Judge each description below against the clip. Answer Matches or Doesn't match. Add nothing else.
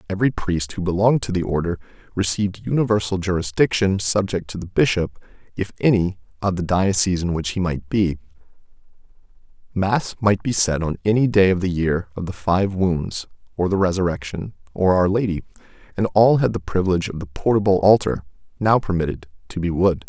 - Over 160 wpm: Matches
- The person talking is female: Doesn't match